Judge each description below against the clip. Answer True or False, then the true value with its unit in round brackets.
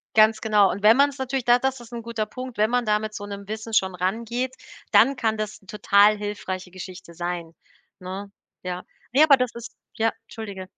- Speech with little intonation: False (3.5 semitones)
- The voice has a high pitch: True (215 Hz)